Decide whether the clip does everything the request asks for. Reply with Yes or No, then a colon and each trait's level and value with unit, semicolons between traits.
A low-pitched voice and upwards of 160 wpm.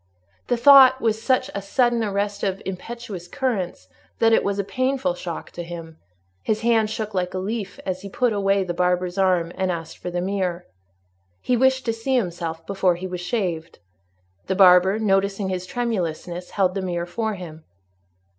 No: high, 195 Hz; average, 180 wpm